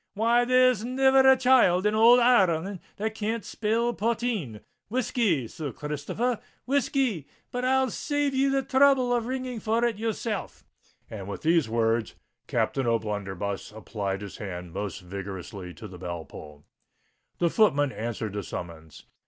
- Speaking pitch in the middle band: No, high, 200 Hz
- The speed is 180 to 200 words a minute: No, average, 145 wpm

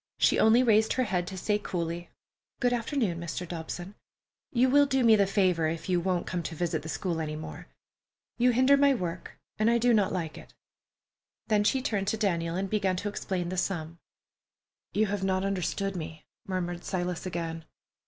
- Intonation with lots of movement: No, average, 4.0 semitones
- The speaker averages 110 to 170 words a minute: No, average, 190 wpm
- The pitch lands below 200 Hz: Yes, high, 190 Hz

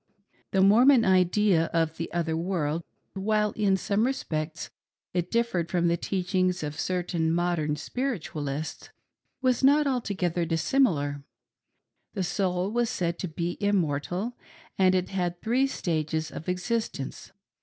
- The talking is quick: No, slow, 135 wpm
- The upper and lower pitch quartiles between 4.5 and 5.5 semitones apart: No, average, 4.1 semitones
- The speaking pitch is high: No, medium, 180 Hz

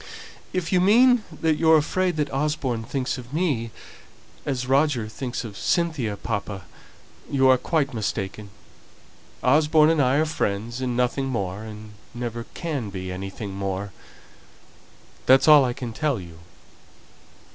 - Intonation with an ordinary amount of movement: No, wide, 6.0 semitones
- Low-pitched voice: Yes, low, 130 Hz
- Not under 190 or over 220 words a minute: No, average, 140 wpm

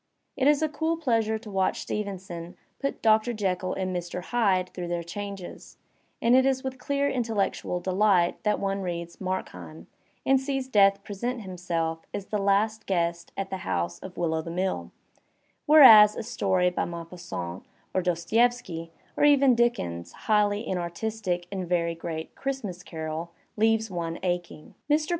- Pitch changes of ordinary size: Yes, average, 4.5 semitones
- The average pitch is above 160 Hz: Yes, high, 190 Hz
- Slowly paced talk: No, average, 155 wpm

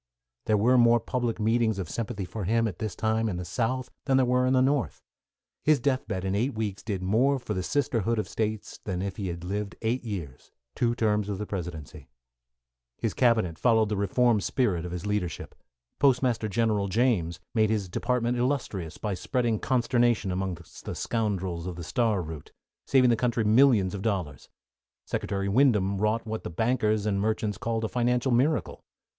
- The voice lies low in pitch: Yes, low, 110 Hz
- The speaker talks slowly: No, average, 185 wpm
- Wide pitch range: No, average, 3.9 semitones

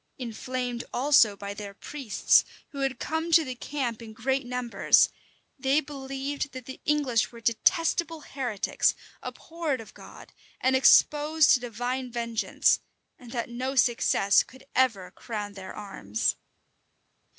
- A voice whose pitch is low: No, very high, 250 Hz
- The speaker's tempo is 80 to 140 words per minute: Yes, slow, 135 wpm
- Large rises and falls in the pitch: No, average, 3.2 semitones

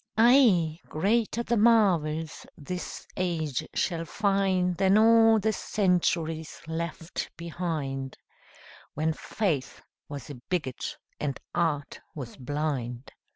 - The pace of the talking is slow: Yes, slow, 105 wpm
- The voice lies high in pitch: No, medium, 170 Hz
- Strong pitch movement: No, average, 4.7 semitones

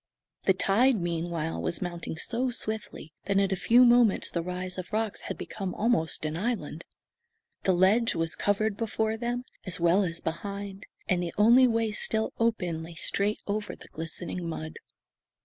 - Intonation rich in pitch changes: No, average, 4.4 semitones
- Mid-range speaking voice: No, high, 195 Hz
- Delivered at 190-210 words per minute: No, average, 165 wpm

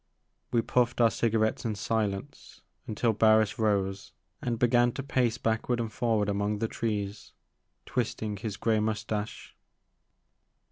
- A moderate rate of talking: No, slow, 130 wpm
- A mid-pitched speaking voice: No, low, 110 Hz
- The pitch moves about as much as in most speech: No, narrow, 2.0 semitones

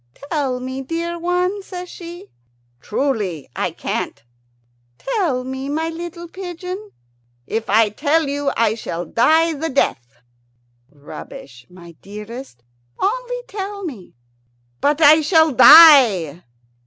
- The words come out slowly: Yes, slow, 115 wpm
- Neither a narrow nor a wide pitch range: No, wide, 7.7 semitones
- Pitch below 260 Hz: No, very high, 285 Hz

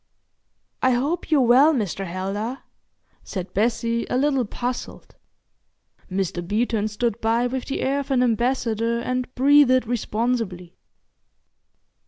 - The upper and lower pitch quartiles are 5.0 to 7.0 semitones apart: No, average, 3.2 semitones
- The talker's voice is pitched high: Yes, high, 240 Hz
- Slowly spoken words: Yes, slow, 120 wpm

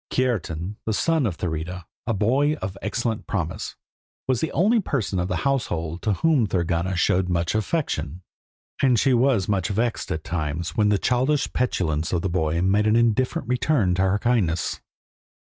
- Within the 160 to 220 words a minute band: Yes, average, 170 wpm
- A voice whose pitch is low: Yes, low, 100 Hz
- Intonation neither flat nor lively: No, wide, 6.0 semitones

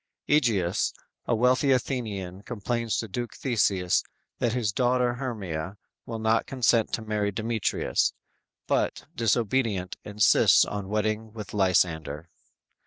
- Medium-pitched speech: No, low, 110 Hz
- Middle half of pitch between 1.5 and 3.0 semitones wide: No, average, 3.7 semitones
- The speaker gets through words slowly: Yes, slow, 120 wpm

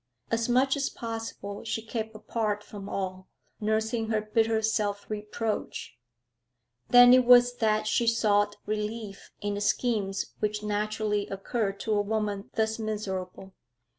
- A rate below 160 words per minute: Yes, slow, 135 wpm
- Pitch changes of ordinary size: No, narrow, 1.7 semitones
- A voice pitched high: Yes, high, 215 Hz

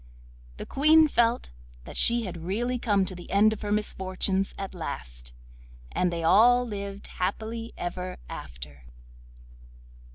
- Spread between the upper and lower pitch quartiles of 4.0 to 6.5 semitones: Yes, average, 4.6 semitones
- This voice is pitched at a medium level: No, high, 195 Hz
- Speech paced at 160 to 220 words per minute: No, slow, 135 wpm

